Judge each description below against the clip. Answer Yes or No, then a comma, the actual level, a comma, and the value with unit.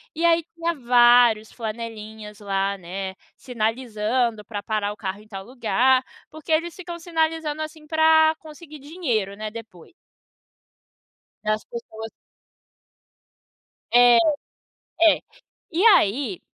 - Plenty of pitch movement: Yes, wide, 6.7 semitones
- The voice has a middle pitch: No, high, 240 Hz